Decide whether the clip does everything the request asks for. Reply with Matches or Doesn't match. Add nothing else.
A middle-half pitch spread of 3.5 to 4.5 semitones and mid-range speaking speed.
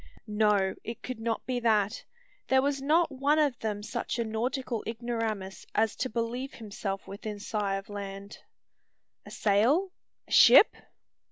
Matches